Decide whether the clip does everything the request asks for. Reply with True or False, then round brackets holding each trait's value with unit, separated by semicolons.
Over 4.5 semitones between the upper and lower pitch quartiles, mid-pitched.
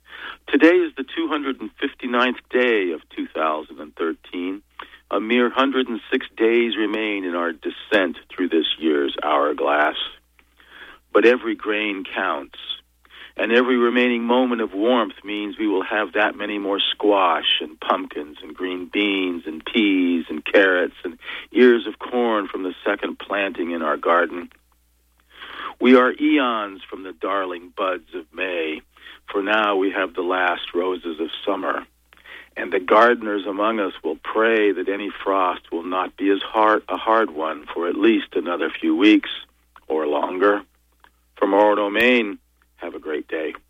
False (5.2 semitones; 105 Hz)